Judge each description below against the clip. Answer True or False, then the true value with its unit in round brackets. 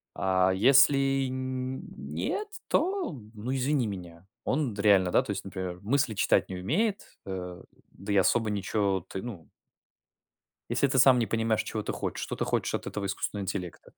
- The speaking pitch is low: True (105 Hz)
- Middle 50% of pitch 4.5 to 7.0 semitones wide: True (5.6 semitones)